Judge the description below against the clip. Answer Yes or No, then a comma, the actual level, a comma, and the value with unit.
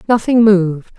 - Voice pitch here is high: Yes, high, 205 Hz